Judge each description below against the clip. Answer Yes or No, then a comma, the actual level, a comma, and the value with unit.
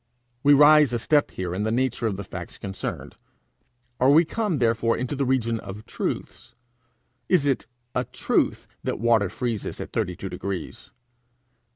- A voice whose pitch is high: No, low, 120 Hz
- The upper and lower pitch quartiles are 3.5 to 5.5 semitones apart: Yes, average, 5.2 semitones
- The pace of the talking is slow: No, average, 165 wpm